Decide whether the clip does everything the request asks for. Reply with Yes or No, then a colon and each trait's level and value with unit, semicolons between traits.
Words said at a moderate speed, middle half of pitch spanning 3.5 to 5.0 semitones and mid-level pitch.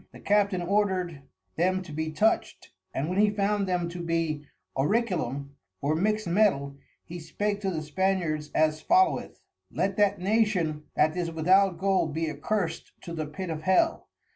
Yes: average, 165 wpm; average, 4.2 semitones; medium, 175 Hz